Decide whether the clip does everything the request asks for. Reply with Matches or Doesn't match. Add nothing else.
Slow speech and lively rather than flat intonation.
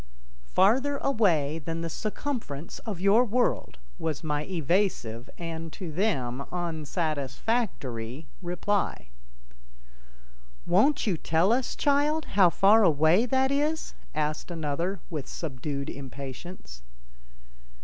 Matches